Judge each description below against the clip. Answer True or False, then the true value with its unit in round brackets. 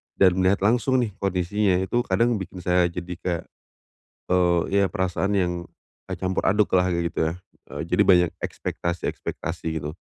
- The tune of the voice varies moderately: False (2.0 semitones)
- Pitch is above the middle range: False (90 Hz)